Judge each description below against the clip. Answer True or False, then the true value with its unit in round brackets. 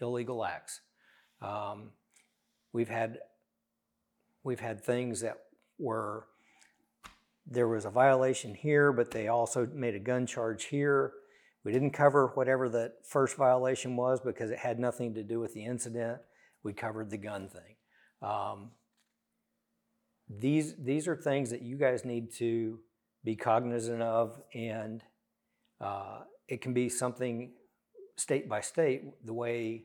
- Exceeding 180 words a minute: False (140 wpm)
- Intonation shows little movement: True (2.3 semitones)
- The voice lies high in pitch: False (120 Hz)